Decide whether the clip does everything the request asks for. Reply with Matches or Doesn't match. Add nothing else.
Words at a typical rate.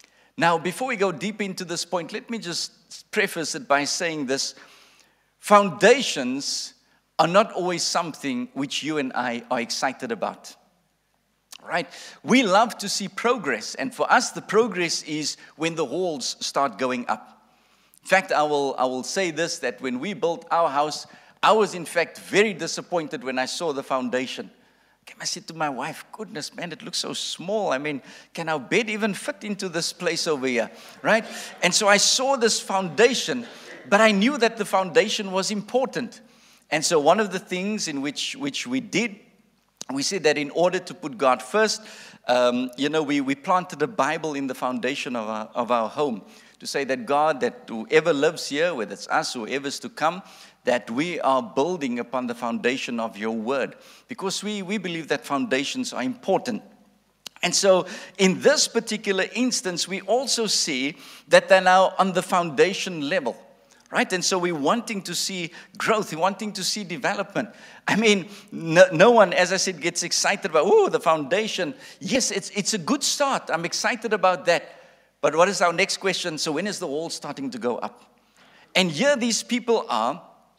Matches